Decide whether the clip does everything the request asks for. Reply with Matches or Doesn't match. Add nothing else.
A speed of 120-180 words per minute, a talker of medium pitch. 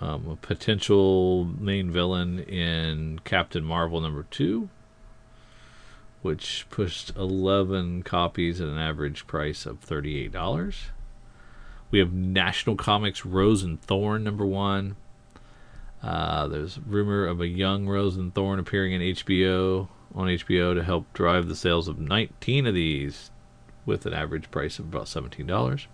Doesn't match